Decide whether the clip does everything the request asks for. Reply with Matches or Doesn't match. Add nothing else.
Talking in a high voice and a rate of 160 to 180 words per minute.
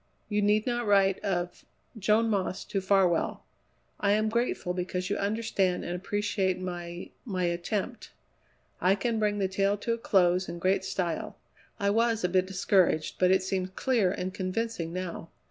Matches